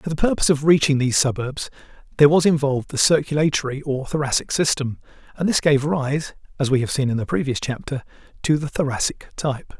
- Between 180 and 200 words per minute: Yes, average, 190 wpm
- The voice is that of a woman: No, male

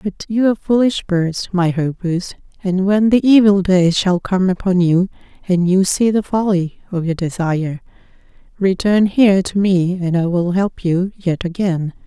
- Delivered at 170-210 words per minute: Yes, average, 175 wpm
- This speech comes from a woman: Yes, female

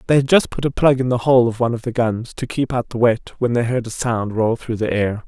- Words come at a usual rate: No, fast, 320 wpm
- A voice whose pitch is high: No, low, 120 Hz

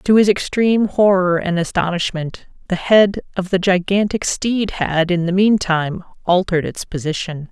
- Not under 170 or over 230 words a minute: No, average, 150 wpm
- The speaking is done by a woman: Yes, female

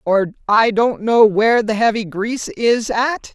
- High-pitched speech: Yes, high, 225 Hz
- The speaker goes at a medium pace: Yes, average, 180 wpm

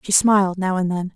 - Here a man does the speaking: No, female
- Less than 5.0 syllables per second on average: No, 5.7 syllables/s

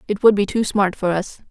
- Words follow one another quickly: Yes, fast, 280 wpm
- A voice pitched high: Yes, high, 200 Hz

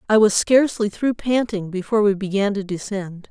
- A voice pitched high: Yes, high, 205 Hz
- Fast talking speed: No, average, 180 wpm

